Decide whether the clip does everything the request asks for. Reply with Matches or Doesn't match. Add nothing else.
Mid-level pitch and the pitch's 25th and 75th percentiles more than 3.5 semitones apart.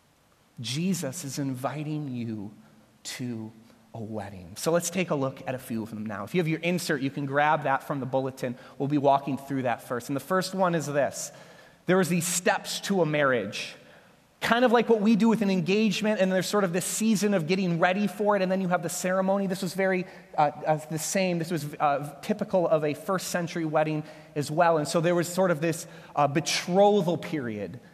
Matches